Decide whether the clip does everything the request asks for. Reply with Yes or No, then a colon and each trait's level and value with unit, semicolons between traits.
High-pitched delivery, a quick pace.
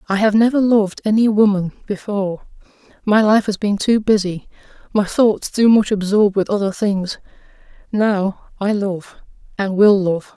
No: high, 205 Hz; average, 155 wpm